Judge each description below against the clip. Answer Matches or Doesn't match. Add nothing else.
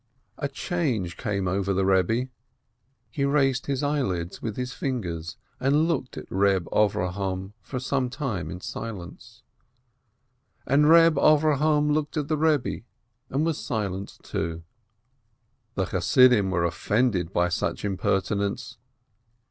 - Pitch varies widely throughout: Matches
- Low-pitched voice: Matches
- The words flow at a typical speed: Doesn't match